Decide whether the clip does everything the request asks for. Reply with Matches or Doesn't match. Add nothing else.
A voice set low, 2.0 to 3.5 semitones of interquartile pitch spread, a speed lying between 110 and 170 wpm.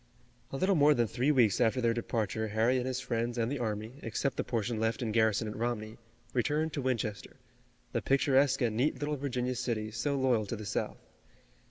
Doesn't match